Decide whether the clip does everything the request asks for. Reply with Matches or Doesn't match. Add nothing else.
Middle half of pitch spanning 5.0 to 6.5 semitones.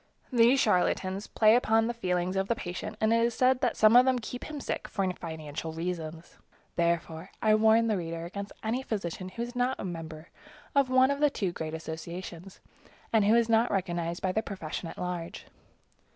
Matches